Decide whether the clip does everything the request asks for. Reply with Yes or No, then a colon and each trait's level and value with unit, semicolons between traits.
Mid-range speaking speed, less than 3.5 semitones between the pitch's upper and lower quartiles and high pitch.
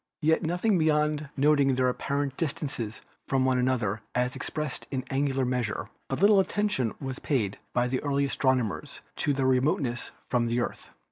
No: average, 155 wpm; average, 3.0 semitones; low, 135 Hz